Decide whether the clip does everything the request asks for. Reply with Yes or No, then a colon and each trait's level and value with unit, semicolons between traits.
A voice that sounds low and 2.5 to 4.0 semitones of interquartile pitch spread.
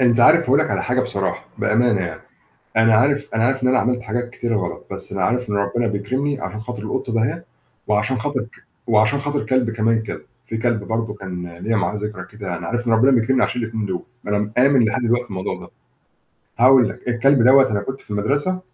Yes: low, 115 Hz; average, 3.2 semitones